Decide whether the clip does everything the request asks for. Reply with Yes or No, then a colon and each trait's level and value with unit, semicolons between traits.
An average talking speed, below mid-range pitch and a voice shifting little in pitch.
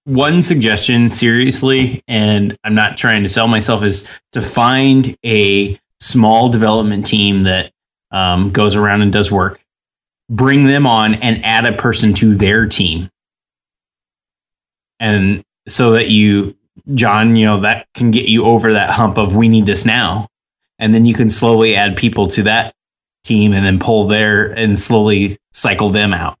Yes: average, 165 wpm; low, 110 Hz; narrow, 2.3 semitones